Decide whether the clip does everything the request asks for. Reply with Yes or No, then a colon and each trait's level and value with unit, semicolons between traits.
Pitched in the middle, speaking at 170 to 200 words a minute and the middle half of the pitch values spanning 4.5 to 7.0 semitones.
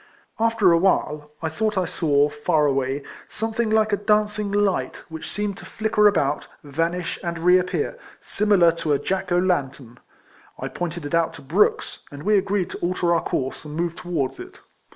Yes: medium, 175 Hz; average, 180 wpm; average, 5.2 semitones